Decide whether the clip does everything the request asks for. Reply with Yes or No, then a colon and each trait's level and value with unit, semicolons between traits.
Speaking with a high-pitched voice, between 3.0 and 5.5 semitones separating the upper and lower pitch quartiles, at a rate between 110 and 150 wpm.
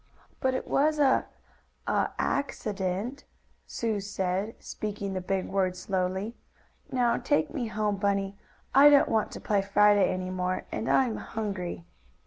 Yes: high, 205 Hz; average, 3.9 semitones; average, 140 wpm